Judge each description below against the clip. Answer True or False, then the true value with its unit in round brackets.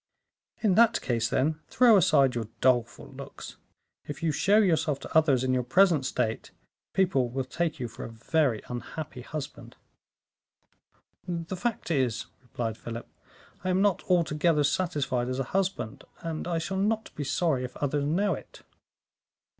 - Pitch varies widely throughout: True (6.0 semitones)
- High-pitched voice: False (150 Hz)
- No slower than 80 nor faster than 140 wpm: False (155 wpm)